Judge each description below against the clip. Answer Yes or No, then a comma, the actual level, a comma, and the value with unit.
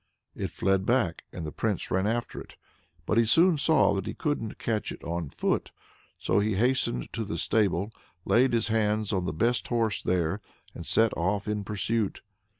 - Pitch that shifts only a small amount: No, average, 3.5 semitones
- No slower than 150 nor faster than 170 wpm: No, average, 185 wpm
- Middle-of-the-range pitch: No, low, 105 Hz